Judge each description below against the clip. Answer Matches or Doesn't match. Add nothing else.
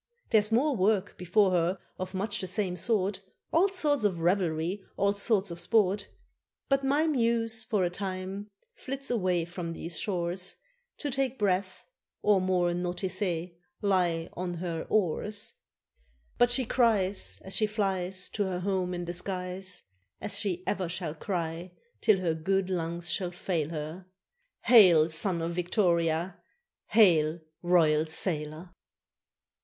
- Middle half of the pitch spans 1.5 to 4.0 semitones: Matches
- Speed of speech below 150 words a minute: Matches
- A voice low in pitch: Doesn't match